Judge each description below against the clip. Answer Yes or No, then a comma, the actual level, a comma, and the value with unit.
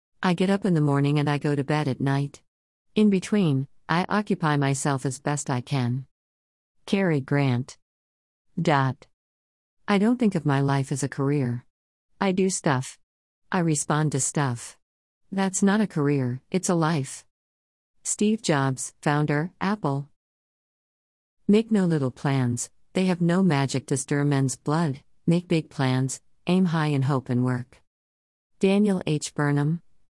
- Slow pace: No, average, 150 wpm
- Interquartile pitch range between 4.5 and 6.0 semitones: Yes, average, 5.3 semitones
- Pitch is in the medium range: Yes, medium, 145 Hz